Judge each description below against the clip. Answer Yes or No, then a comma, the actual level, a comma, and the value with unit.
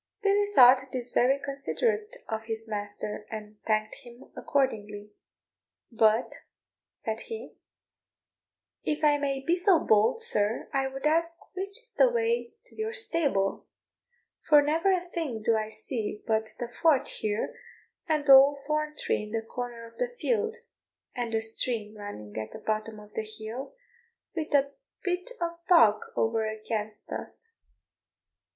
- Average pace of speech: Yes, average, 150 wpm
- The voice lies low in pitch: No, very high, 255 Hz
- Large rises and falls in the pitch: Yes, wide, 7.4 semitones